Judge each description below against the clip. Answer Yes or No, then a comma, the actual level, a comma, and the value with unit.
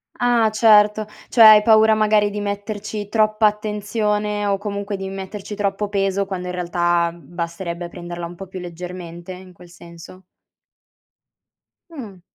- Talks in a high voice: Yes, high, 200 Hz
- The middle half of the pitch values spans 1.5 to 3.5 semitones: Yes, average, 2.9 semitones